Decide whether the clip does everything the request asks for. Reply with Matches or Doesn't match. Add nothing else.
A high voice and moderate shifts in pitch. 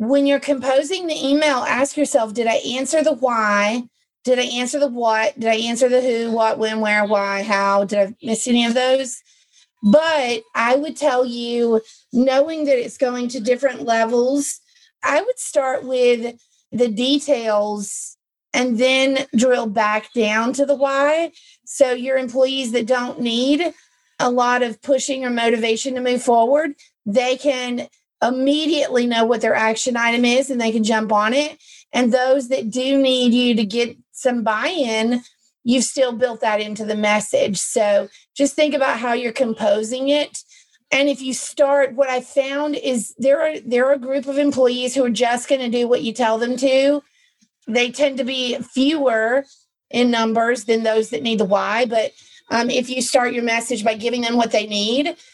Matches